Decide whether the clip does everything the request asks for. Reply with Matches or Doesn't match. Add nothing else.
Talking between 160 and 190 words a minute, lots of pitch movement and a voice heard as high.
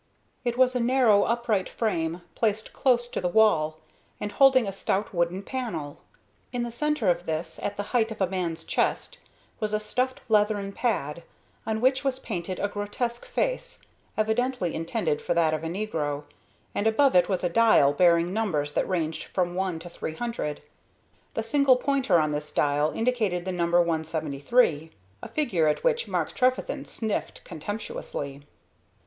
Matches